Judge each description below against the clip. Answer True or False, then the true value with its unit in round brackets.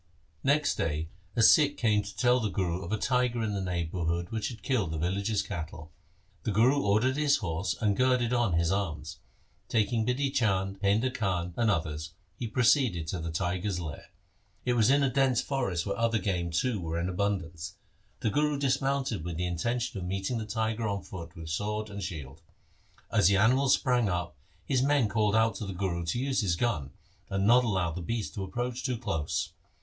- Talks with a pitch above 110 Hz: False (105 Hz)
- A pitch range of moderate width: False (5.7 semitones)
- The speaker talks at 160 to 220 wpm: True (200 wpm)